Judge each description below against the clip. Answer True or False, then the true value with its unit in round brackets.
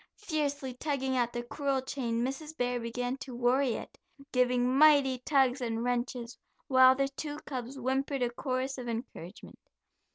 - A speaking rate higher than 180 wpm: False (155 wpm)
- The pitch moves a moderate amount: False (2.0 semitones)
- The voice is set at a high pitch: True (255 Hz)